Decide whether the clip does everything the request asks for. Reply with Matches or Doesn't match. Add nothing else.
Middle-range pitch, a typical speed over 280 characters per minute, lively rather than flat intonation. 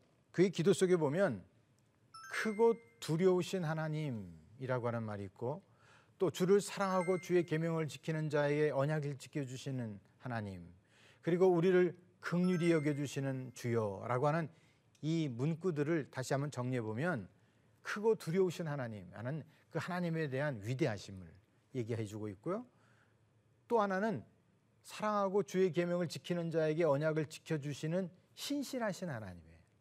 Matches